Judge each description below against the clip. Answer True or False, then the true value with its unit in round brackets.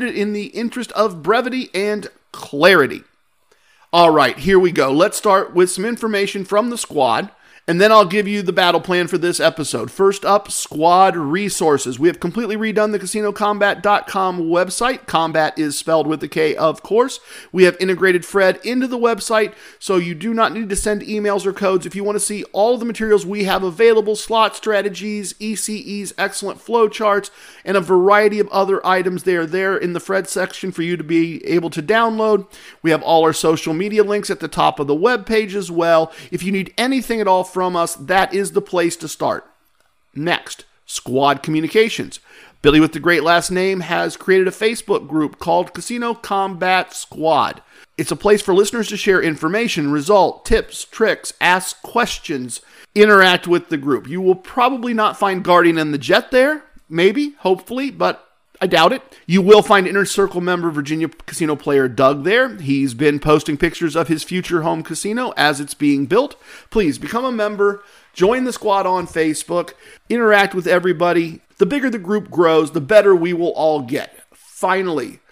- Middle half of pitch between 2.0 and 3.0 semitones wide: False (3.8 semitones)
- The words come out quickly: False (185 wpm)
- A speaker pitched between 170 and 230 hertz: True (190 Hz)